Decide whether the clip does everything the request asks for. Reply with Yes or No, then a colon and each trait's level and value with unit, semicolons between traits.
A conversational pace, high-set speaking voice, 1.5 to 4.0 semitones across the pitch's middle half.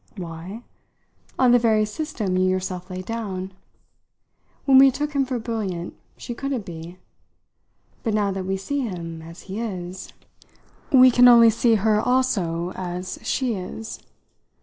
No: average, 150 wpm; high, 205 Hz; average, 4.8 semitones